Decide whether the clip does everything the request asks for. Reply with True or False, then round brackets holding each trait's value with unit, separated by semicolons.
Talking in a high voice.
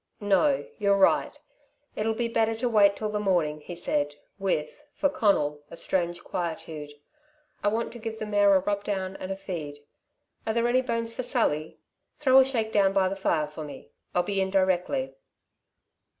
True (200 Hz)